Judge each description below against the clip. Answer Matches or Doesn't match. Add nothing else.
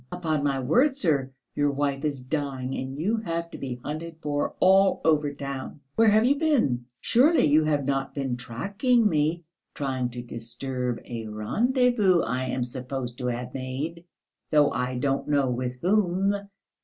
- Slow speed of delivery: Doesn't match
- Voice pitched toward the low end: Doesn't match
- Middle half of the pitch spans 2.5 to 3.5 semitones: Doesn't match